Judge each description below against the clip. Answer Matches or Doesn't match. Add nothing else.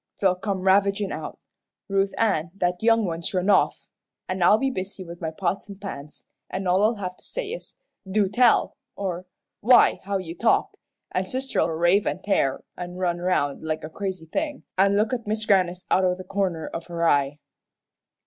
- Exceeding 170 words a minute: Matches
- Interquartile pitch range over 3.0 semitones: Doesn't match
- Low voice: Doesn't match